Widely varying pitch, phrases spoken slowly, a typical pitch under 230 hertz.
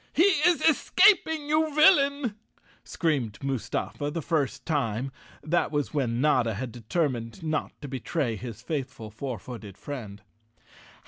Yes: wide, 7.1 semitones; slow, 125 wpm; medium, 140 Hz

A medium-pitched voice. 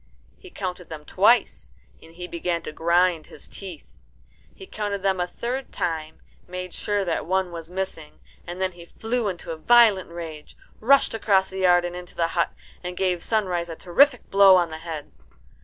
Yes: medium, 180 Hz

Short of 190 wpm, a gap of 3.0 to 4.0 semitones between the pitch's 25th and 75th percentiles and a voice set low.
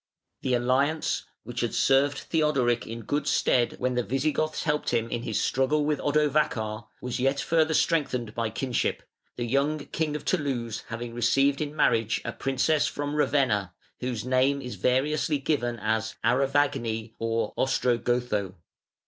Yes: average, 150 wpm; average, 3.7 semitones; low, 130 Hz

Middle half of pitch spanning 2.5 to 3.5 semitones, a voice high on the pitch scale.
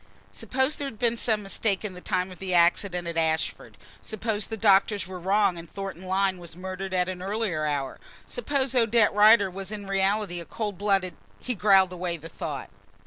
Yes: average, 2.9 semitones; high, 195 Hz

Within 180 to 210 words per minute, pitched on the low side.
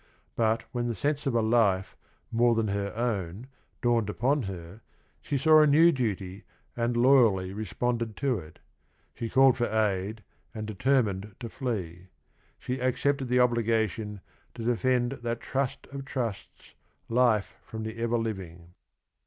No: average, 160 wpm; low, 115 Hz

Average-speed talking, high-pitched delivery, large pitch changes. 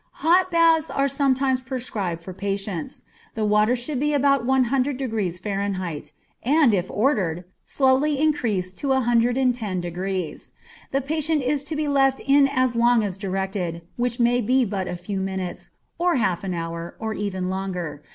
Yes: average, 160 wpm; high, 235 Hz; wide, 6.3 semitones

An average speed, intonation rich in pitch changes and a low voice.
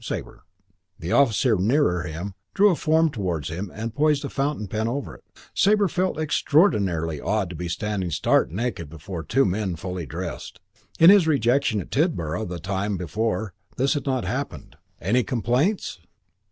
Yes: average, 165 wpm; wide, 7.8 semitones; low, 110 Hz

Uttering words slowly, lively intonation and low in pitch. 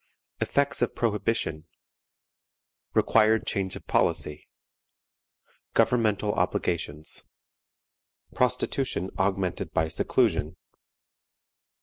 Yes: slow, 65 wpm; wide, 5.7 semitones; low, 100 Hz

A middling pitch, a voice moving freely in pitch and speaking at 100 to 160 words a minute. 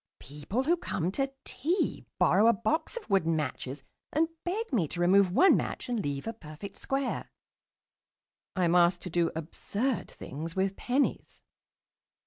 No: high, 195 Hz; wide, 8.3 semitones; average, 155 wpm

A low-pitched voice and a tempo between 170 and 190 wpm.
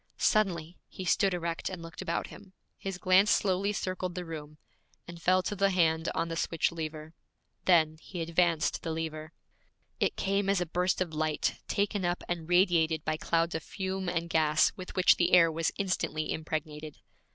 No: medium, 170 Hz; average, 180 wpm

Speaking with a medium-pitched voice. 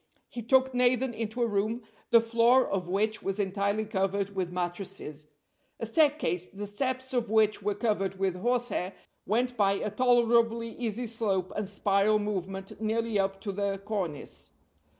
No: high, 210 Hz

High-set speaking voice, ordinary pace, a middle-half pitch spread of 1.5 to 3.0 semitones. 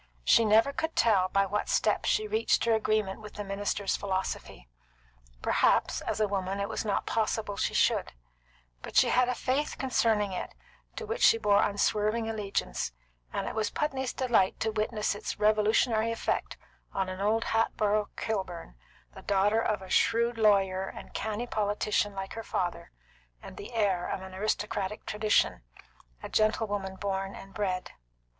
Yes: high, 210 Hz; average, 165 wpm; narrow, 2.4 semitones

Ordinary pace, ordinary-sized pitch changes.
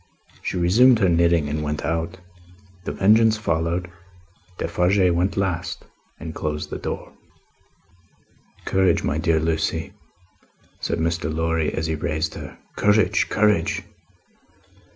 No: slow, 120 wpm; average, 3.0 semitones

